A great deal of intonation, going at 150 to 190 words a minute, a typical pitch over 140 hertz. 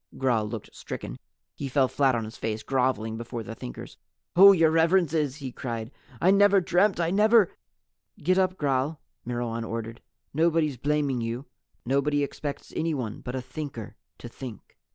No: wide, 5.7 semitones; average, 160 wpm; low, 135 Hz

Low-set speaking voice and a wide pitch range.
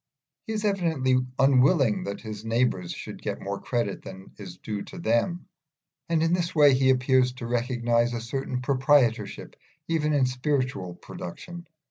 No: low, 130 Hz; average, 4.3 semitones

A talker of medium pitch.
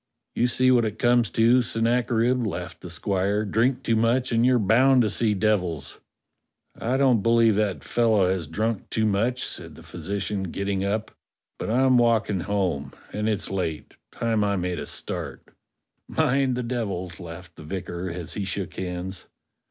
No: low, 105 Hz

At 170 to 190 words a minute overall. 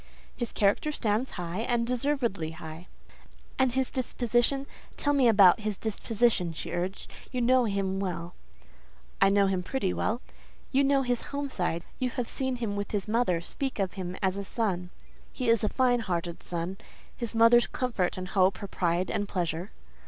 Yes: average, 175 wpm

